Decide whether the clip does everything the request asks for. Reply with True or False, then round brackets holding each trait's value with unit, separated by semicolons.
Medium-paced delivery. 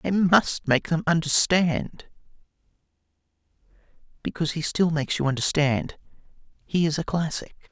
False (115 wpm)